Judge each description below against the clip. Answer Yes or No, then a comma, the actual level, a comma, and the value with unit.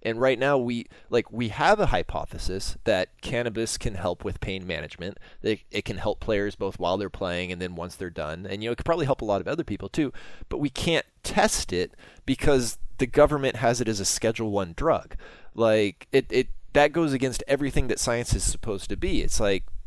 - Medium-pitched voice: No, low, 115 Hz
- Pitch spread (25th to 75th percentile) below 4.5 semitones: No, wide, 5.5 semitones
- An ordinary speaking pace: No, fast, 220 wpm